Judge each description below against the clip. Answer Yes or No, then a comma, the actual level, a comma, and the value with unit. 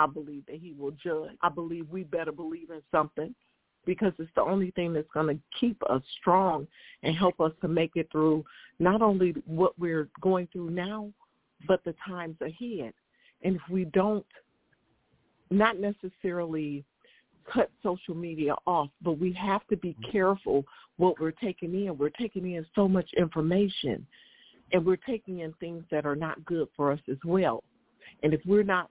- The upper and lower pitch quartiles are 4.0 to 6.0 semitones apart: No, average, 3.2 semitones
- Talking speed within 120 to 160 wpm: No, average, 175 wpm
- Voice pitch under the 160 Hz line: No, medium, 175 Hz